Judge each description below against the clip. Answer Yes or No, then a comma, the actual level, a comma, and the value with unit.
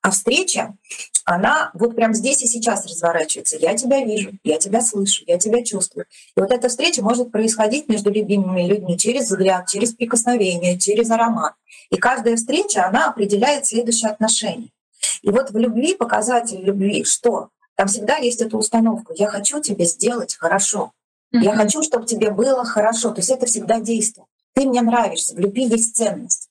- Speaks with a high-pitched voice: Yes, high, 225 Hz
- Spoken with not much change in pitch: No, average, 3.0 semitones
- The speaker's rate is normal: No, fast, 170 wpm